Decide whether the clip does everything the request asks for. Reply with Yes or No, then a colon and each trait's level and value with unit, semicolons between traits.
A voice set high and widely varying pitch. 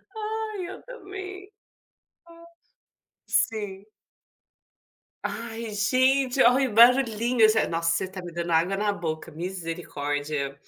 Yes: high, 215 Hz; wide, 7.7 semitones